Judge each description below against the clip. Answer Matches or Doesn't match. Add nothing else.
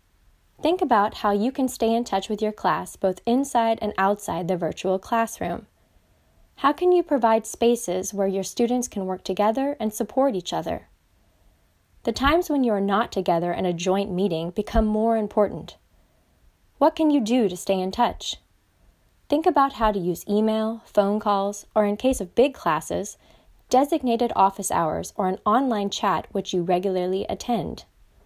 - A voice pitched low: Doesn't match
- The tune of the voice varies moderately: Matches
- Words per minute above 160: Matches